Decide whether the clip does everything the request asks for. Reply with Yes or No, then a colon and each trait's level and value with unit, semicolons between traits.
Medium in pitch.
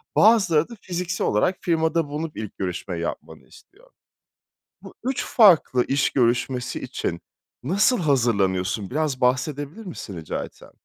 Yes: medium, 145 Hz